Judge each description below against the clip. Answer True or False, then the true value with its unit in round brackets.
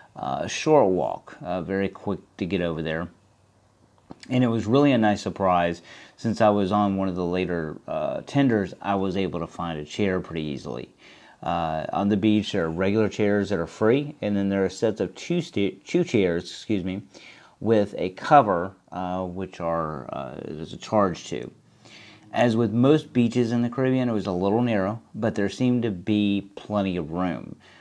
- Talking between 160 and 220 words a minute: True (195 wpm)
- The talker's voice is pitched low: True (100 Hz)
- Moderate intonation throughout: True (3.7 semitones)